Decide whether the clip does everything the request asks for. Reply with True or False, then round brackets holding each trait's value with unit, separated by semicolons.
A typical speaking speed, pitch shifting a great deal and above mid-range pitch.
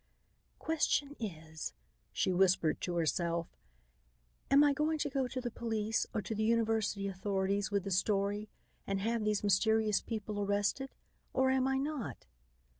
False (150 wpm; 4.2 semitones; 215 Hz)